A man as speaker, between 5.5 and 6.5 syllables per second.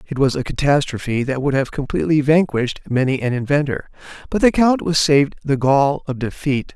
Yes: male; 5.7 syllables/s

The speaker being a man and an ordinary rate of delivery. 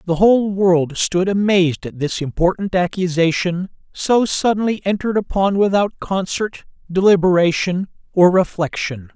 No: male; slow, 120 wpm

